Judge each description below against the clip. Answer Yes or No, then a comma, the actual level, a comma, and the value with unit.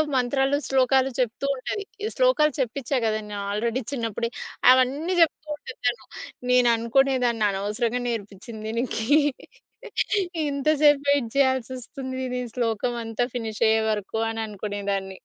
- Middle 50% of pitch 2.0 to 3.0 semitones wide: No, average, 3.4 semitones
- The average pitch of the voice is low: No, high, 245 Hz